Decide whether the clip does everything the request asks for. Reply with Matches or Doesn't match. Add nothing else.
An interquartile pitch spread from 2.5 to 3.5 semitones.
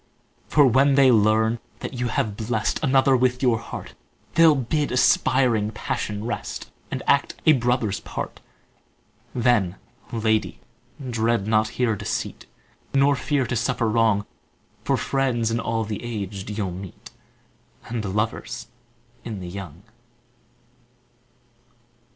Matches